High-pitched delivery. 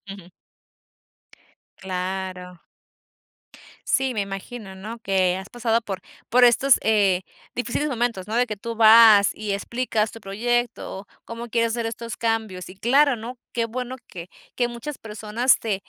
Yes: high, 225 Hz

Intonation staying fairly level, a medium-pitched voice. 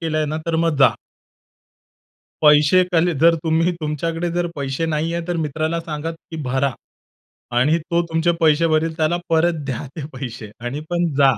Yes: narrow, 2.1 semitones; medium, 160 Hz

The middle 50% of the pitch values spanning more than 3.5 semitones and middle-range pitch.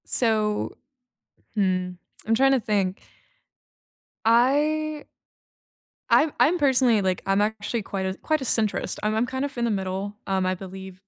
No: wide, 5.5 semitones; high, 215 Hz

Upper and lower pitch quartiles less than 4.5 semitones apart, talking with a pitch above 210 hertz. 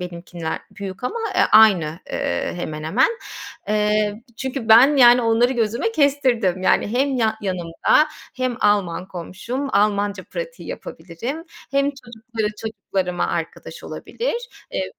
No: wide, 5.5 semitones; high, 220 Hz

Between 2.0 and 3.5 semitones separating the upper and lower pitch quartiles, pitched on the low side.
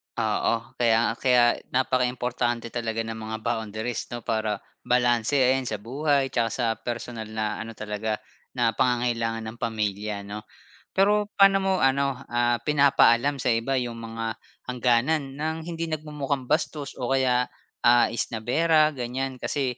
Yes: average, 3.2 semitones; low, 120 Hz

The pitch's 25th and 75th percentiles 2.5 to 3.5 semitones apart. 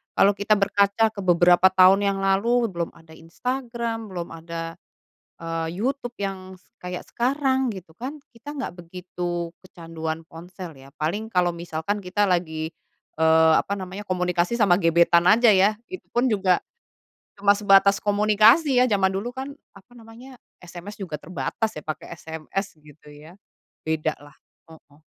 No: average, 4.3 semitones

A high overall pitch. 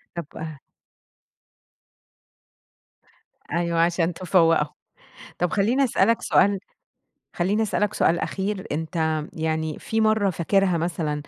No: medium, 175 Hz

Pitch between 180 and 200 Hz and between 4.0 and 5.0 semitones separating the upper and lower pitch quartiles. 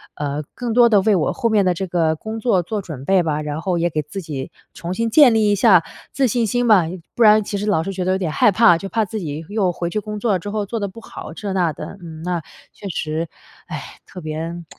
Yes: high, 190 Hz; average, 4.6 semitones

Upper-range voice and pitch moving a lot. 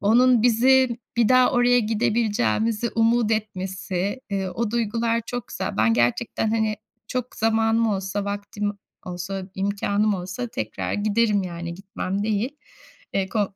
No: high, 215 Hz; average, 3.0 semitones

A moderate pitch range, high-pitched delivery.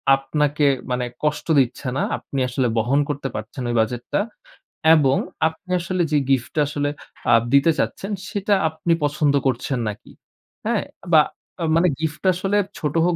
No: average, 3.5 semitones; medium, 145 Hz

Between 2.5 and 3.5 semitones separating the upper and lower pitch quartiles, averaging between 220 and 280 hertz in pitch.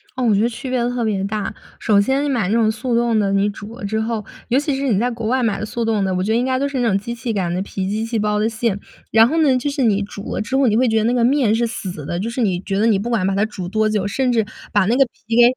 Yes: average, 3.0 semitones; high, 225 Hz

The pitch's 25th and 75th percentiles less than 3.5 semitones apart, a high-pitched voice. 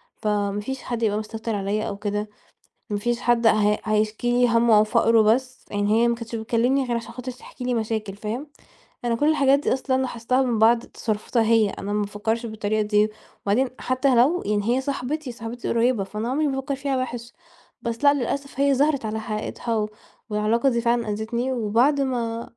Yes: average, 3.0 semitones; high, 235 Hz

